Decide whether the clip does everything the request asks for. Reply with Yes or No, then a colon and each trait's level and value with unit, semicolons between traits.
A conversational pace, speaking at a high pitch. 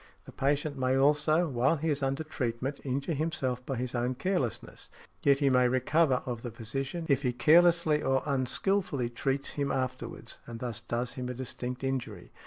No: average, 180 wpm; low, 135 Hz